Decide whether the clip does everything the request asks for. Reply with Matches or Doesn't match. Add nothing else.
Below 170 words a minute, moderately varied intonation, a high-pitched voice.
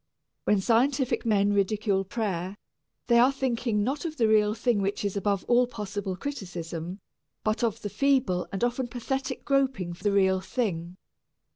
Matches